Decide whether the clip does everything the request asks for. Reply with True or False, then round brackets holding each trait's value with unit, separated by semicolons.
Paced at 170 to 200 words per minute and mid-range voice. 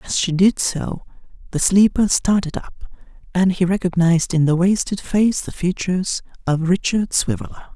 False (155 wpm; 180 Hz)